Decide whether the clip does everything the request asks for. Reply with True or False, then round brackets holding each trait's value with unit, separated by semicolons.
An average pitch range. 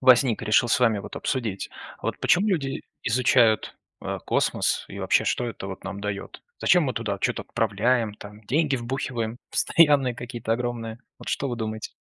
True (3.0 semitones)